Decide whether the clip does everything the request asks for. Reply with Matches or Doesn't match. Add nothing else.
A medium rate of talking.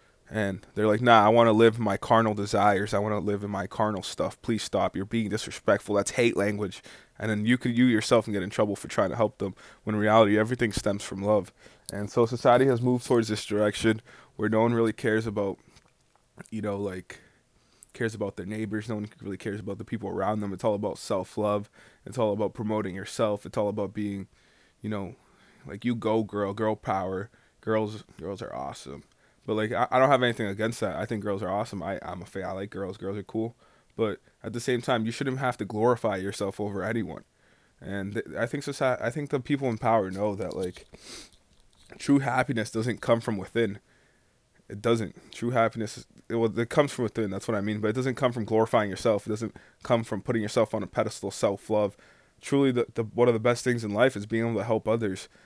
Doesn't match